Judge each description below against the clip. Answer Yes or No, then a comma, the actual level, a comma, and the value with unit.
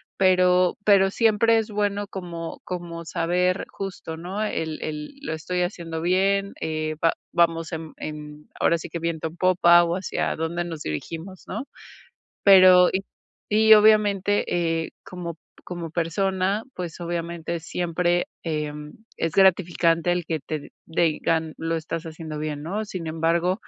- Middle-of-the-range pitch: Yes, medium, 170 Hz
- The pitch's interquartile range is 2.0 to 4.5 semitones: Yes, narrow, 2.6 semitones